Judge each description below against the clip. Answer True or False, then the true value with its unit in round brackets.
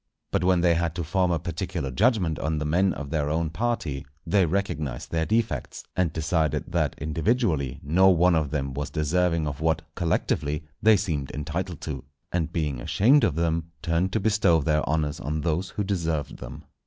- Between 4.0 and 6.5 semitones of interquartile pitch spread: False (3.2 semitones)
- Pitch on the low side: True (80 Hz)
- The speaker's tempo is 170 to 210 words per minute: True (185 wpm)